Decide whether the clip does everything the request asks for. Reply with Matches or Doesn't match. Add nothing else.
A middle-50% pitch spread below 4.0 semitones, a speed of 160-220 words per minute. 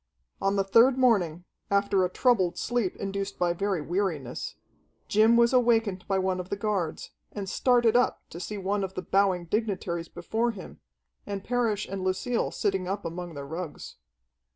Matches